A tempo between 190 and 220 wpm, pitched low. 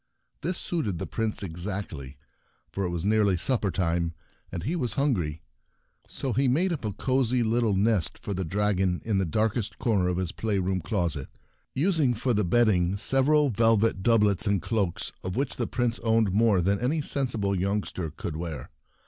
No: average, 170 wpm; low, 105 Hz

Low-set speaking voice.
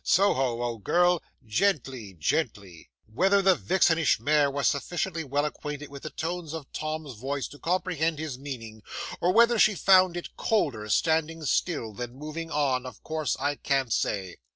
No: medium, 150 Hz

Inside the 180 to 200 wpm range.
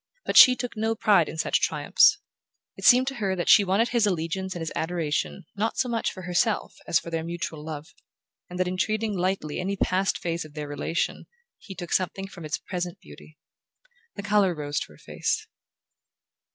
Yes: average, 195 wpm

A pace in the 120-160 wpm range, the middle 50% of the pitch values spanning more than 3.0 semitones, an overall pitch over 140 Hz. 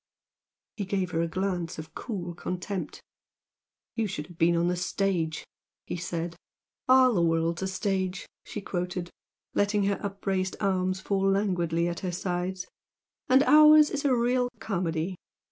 No: average, 150 wpm; average, 2.7 semitones; medium, 185 Hz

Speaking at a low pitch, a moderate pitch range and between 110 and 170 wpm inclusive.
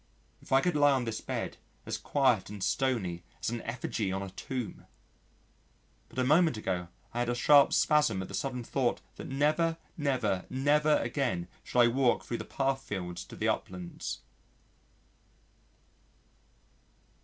Yes: low, 125 Hz; average, 5.0 semitones; average, 155 wpm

